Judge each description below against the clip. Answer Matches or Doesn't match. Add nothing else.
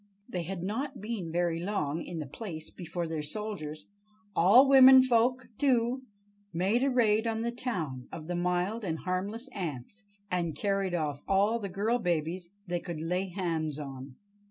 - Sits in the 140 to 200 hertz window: Matches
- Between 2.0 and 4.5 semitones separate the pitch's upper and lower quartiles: Doesn't match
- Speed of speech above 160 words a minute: Doesn't match